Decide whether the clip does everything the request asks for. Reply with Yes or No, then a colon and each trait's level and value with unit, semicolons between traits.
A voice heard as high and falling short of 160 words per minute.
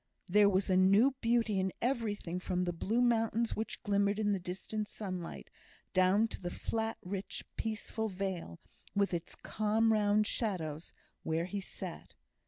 Yes: high, 200 Hz; average, 150 wpm